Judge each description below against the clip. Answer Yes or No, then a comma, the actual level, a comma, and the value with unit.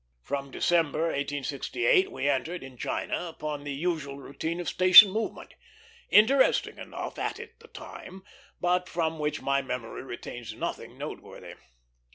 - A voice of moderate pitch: Yes, medium, 155 Hz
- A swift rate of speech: No, slow, 135 wpm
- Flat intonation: No, average, 4.5 semitones